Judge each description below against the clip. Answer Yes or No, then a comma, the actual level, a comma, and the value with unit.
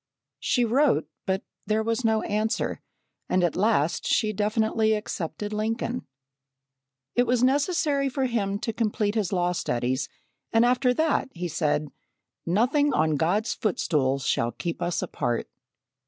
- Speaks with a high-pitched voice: Yes, high, 215 Hz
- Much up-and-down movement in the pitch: Yes, wide, 5.8 semitones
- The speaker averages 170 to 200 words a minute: No, average, 140 wpm